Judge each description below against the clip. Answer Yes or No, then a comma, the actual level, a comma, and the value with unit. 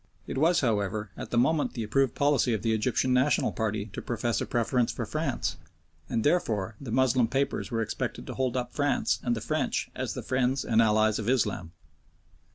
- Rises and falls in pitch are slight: No, average, 3.1 semitones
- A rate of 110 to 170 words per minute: No, average, 195 wpm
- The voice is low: Yes, low, 120 Hz